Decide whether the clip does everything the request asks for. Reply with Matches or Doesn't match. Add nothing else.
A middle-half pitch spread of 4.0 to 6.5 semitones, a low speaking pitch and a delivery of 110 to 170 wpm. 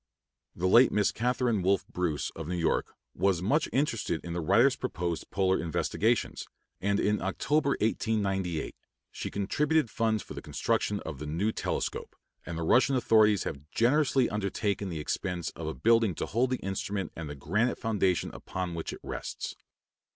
Matches